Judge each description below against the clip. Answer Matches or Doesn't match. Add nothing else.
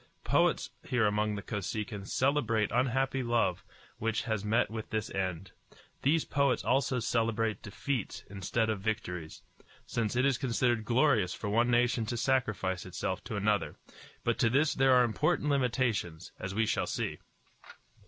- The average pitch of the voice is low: Matches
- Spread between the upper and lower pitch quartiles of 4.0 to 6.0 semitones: Doesn't match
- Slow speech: Doesn't match